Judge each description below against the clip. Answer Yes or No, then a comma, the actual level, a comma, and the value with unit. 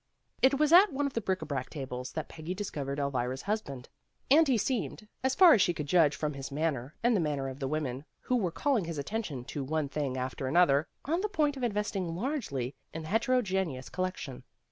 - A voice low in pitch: No, medium, 165 Hz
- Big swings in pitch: Yes, wide, 8.8 semitones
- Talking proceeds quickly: Yes, fast, 215 wpm